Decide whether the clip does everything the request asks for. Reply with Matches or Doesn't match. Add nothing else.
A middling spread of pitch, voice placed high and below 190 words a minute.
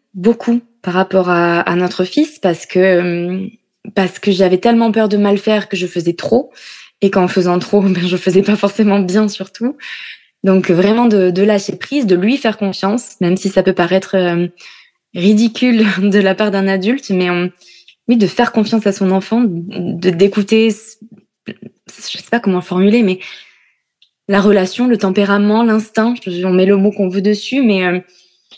Matches